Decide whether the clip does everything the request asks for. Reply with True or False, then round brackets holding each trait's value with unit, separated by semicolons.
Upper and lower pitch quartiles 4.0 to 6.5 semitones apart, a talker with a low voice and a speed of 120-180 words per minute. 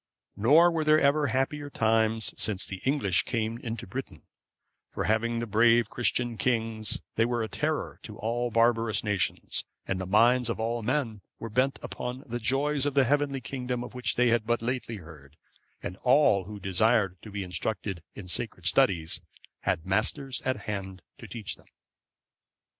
False (3.5 semitones; 115 Hz; 170 wpm)